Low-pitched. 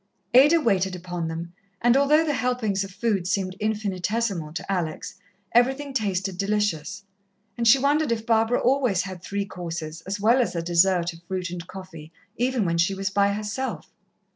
No: high, 200 Hz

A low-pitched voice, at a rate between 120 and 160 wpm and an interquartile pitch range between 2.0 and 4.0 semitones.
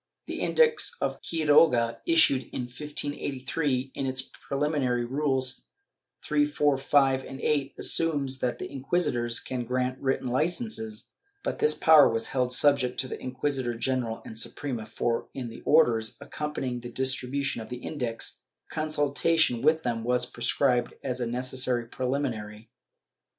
Yes: low, 130 Hz; average, 140 wpm; average, 3.0 semitones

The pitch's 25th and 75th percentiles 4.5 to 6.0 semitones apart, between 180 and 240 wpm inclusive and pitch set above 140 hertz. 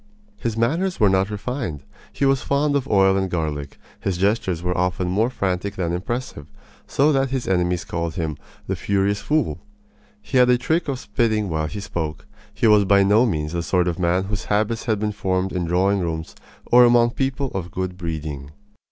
No: average, 5.1 semitones; average, 195 wpm; very low, 95 Hz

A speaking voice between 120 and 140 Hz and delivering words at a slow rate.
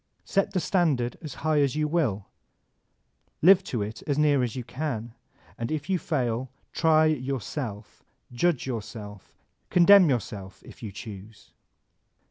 No: low, 135 Hz; average, 150 wpm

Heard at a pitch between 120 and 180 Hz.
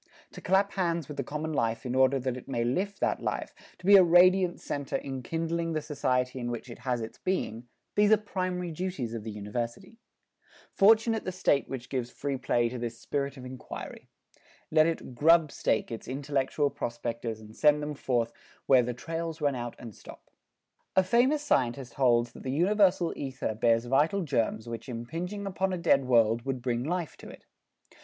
Yes: medium, 140 Hz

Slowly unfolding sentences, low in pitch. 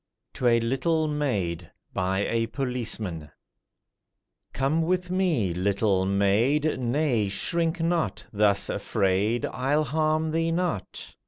Yes: slow, 110 wpm; low, 125 Hz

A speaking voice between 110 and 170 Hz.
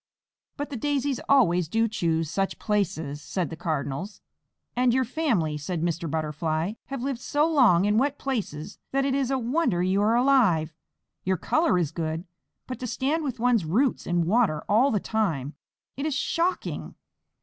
No: high, 215 Hz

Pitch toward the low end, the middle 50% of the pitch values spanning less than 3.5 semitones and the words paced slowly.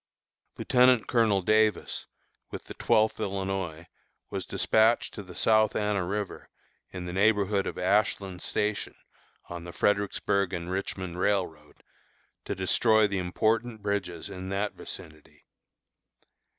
Yes: low, 100 Hz; average, 3.0 semitones; slow, 125 wpm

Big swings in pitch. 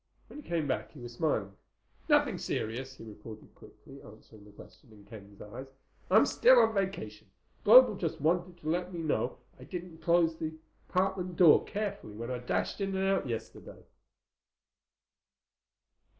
Yes: wide, 8.4 semitones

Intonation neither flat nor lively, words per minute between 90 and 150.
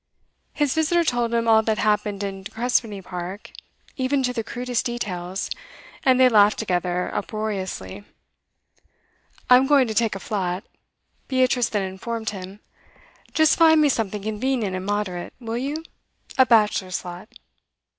Yes: average, 4.5 semitones; average, 145 wpm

